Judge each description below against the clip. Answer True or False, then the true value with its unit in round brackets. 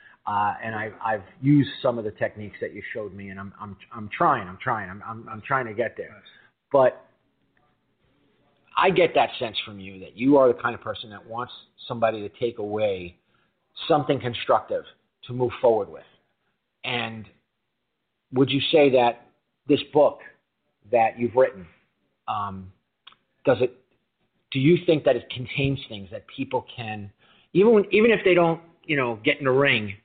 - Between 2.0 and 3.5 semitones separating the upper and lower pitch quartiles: False (4.7 semitones)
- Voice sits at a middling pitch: False (120 Hz)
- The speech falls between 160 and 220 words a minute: True (175 wpm)